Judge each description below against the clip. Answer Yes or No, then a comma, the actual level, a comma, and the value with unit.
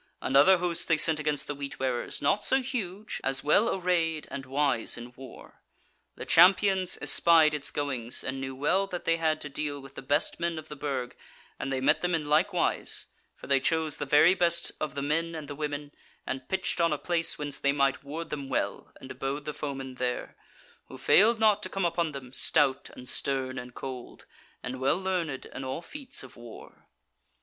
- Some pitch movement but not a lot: Yes, average, 4.0 semitones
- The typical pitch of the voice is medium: Yes, medium, 150 Hz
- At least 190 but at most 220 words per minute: Yes, fast, 205 wpm